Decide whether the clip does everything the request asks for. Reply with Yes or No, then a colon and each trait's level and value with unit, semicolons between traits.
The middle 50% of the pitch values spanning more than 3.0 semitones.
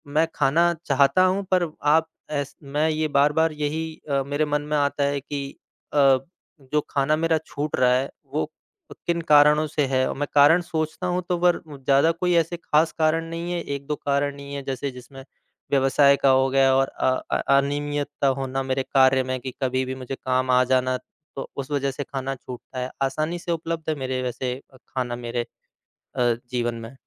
No: average, 2.7 semitones